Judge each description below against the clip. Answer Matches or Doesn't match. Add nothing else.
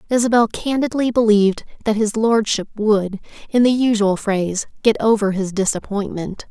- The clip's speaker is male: Doesn't match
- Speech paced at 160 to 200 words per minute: Doesn't match